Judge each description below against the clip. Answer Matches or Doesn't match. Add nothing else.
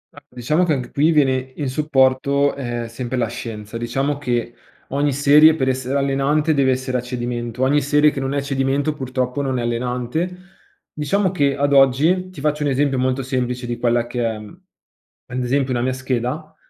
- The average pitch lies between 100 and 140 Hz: Matches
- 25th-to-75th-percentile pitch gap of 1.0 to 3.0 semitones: Matches